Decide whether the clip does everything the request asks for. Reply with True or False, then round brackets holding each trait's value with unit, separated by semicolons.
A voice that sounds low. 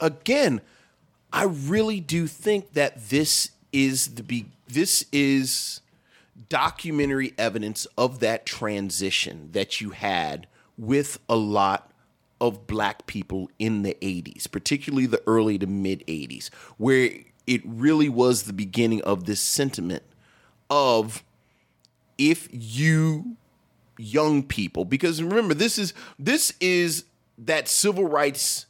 True (130 Hz)